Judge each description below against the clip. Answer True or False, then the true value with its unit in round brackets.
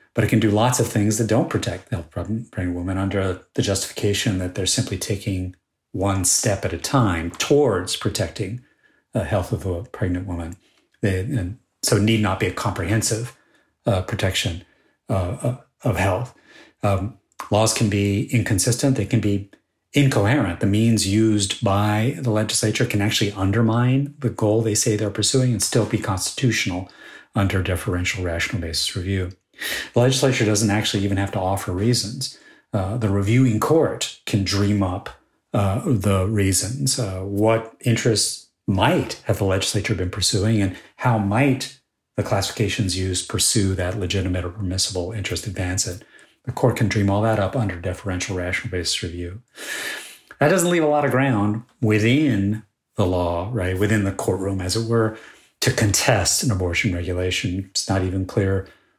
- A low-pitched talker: True (105 Hz)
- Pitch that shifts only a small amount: False (3.4 semitones)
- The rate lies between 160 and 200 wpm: True (165 wpm)